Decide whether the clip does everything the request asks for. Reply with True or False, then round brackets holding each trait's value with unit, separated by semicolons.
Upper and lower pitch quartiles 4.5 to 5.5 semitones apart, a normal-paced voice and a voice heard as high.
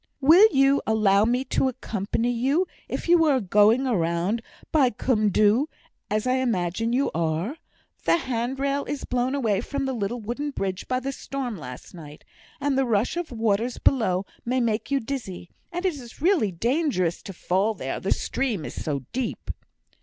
True (5.1 semitones; 180 wpm; 240 Hz)